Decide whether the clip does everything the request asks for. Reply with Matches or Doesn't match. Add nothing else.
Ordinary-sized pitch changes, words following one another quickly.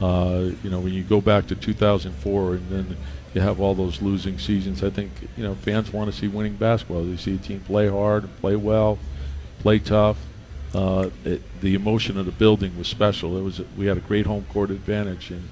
Doesn't match